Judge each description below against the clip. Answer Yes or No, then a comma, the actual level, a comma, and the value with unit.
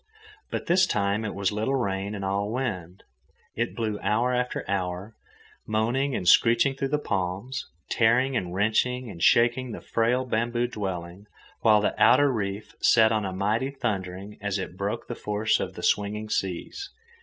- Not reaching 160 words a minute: No, average, 165 wpm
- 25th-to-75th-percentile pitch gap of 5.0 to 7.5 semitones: No, average, 3.7 semitones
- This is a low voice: Yes, low, 110 Hz